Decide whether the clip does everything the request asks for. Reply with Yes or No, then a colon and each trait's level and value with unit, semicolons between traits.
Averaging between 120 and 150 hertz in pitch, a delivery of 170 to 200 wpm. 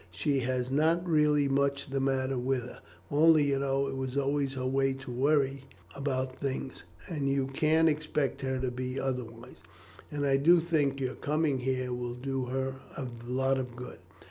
Yes: low, 135 Hz; average, 180 wpm